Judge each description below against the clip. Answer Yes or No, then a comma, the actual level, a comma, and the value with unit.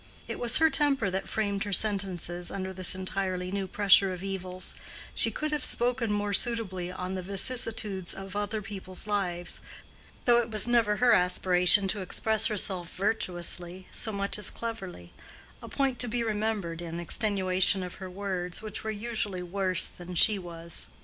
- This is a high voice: Yes, high, 195 Hz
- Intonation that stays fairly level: No, average, 3.1 semitones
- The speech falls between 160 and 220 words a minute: Yes, average, 165 wpm